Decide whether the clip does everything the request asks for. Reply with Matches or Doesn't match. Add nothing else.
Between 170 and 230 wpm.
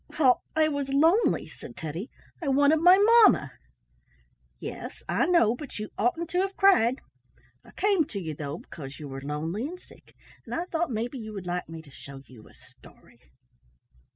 Matches